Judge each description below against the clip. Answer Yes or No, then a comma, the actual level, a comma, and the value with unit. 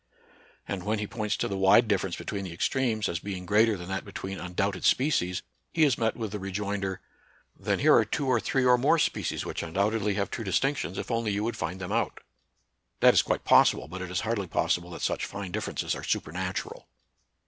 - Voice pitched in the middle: No, low, 100 Hz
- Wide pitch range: No, average, 3.3 semitones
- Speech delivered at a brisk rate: Yes, fast, 215 wpm